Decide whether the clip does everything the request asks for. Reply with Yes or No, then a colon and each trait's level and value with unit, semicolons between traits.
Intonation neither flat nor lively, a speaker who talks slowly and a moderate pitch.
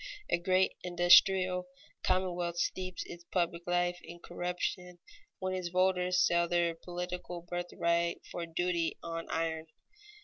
No: narrow, 0.9 semitones; slow, 130 wpm; medium, 175 Hz